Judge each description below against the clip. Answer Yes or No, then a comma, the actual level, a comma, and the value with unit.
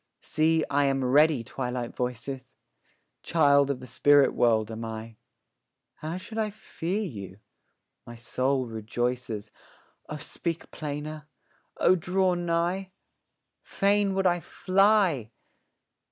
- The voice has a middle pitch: Yes, medium, 145 Hz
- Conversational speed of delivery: No, slow, 115 wpm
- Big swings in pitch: Yes, wide, 6.2 semitones